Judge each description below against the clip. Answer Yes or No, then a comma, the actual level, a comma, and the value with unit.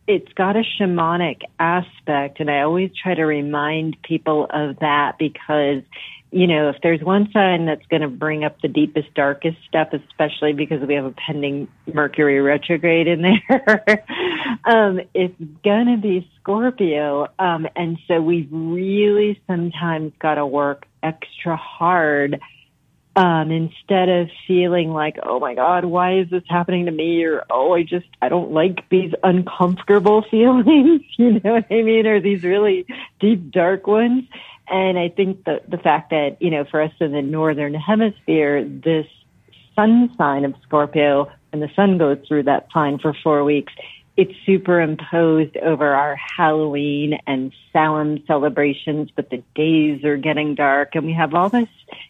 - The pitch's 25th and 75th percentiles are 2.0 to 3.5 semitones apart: No, average, 3.9 semitones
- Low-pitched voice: No, medium, 165 Hz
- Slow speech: No, average, 160 wpm